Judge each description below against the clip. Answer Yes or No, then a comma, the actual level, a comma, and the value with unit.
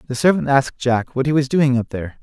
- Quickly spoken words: Yes, fast, 270 wpm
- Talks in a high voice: No, low, 130 Hz